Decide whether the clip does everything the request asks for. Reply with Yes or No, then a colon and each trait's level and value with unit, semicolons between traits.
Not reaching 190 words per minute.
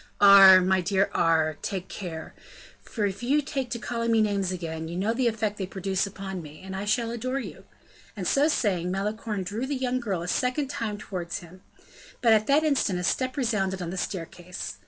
No: average, 200 wpm